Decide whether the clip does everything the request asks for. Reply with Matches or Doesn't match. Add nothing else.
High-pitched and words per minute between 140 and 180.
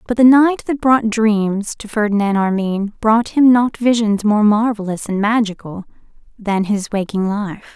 Matches